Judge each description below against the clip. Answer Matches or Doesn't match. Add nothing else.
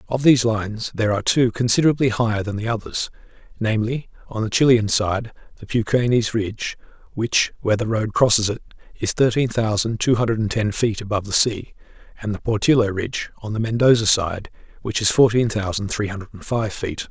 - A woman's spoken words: Doesn't match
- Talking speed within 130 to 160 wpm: Doesn't match